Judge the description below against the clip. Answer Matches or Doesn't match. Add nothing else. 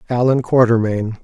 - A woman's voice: Doesn't match